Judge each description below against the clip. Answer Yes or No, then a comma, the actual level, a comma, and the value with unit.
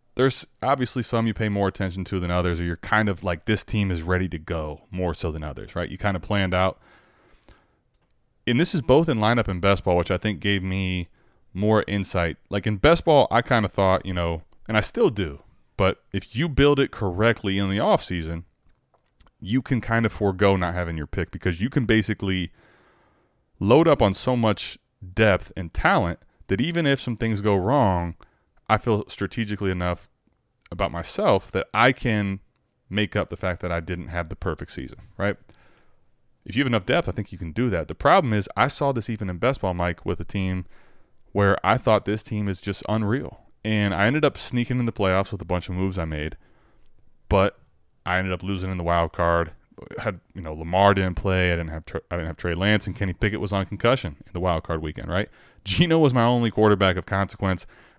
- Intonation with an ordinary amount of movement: Yes, average, 3.6 semitones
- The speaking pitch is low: Yes, low, 100 Hz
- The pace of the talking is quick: Yes, fast, 220 wpm